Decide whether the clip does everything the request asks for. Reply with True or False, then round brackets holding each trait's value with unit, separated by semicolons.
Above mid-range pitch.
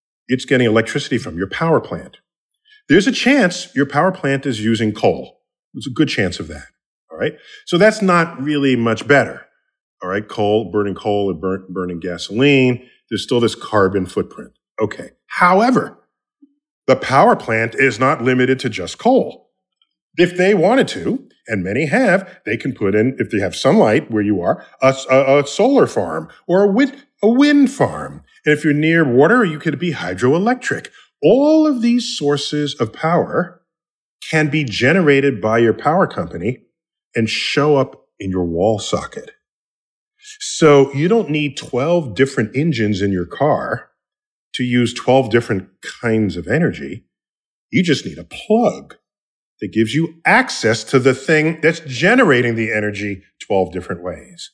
False (135 Hz)